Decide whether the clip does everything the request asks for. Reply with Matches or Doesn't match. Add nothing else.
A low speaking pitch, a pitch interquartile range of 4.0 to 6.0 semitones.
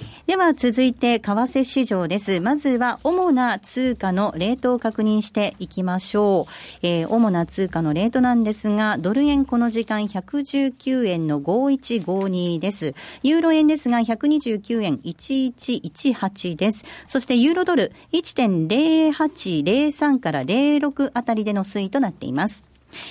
Doesn't match